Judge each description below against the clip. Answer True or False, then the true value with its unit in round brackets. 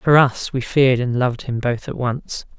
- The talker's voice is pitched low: True (125 Hz)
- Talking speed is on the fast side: True (230 wpm)